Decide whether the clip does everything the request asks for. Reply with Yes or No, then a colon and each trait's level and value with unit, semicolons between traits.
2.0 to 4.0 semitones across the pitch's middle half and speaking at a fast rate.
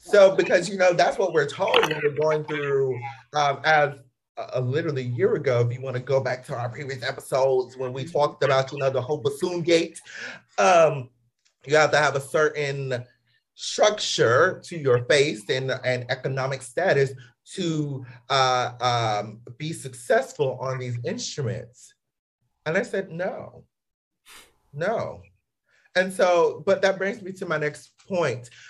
No: average, 3.6 semitones; average, 165 wpm